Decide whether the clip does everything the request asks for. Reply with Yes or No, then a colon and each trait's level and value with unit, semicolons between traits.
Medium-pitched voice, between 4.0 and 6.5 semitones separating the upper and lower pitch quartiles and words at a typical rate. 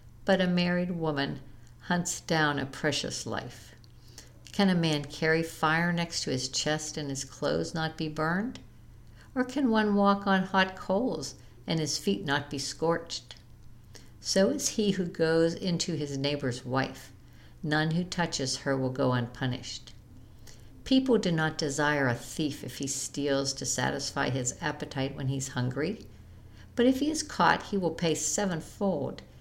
Yes: medium, 150 Hz; average, 5.2 semitones; average, 160 wpm